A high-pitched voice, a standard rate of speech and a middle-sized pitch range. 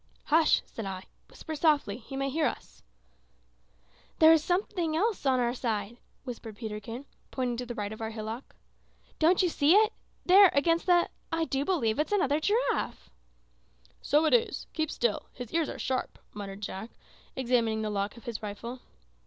No: very high, 260 Hz; average, 170 wpm; wide, 6.5 semitones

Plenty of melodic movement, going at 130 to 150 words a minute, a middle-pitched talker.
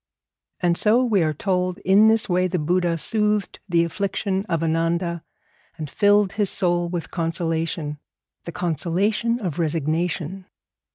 No: average, 3.2 semitones; slow, 135 wpm; medium, 175 Hz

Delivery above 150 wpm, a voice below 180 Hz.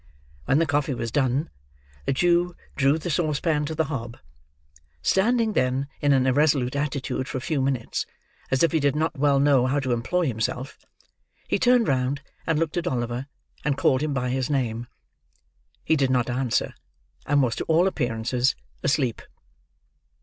Yes: average, 170 wpm; medium, 140 Hz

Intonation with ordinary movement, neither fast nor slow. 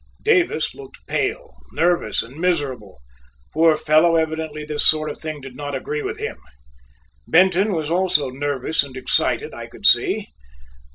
Yes: average, 3.5 semitones; average, 150 wpm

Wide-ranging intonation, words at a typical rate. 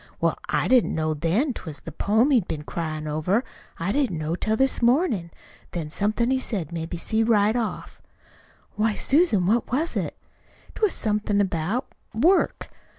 Yes: wide, 6.6 semitones; average, 175 wpm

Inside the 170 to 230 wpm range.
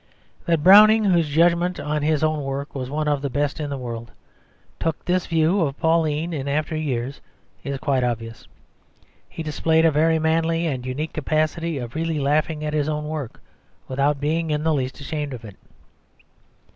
Yes: average, 180 wpm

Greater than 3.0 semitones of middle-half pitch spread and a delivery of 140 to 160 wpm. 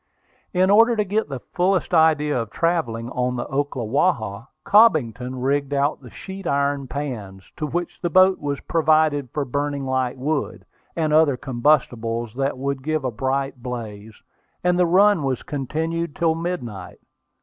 Yes: average, 4.7 semitones; average, 155 wpm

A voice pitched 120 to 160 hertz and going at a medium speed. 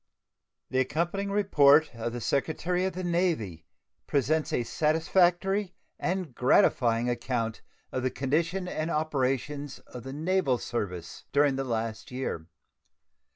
No: medium, 140 Hz; slow, 125 wpm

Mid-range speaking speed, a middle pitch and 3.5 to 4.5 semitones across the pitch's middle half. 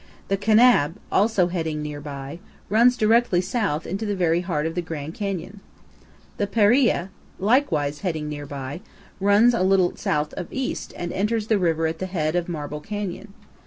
No: average, 170 wpm; medium, 180 Hz; average, 5.2 semitones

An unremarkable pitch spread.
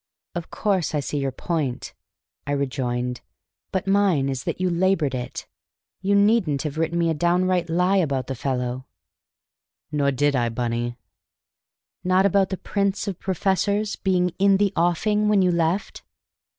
No: wide, 5.8 semitones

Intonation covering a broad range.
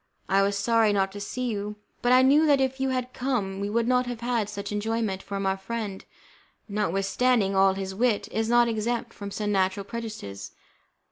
No: average, 3.5 semitones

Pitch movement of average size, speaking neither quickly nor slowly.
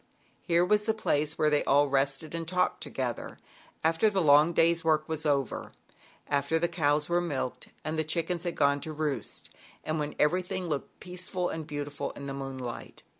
Yes: average, 3.1 semitones; average, 180 wpm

